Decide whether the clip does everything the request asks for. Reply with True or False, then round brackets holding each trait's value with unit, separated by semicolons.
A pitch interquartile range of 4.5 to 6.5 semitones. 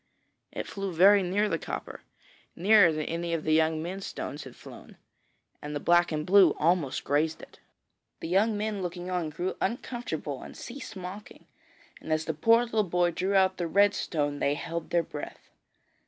False (3.9 semitones)